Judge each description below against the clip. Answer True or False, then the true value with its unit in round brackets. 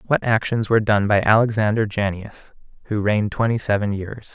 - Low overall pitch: True (105 Hz)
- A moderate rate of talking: True (165 wpm)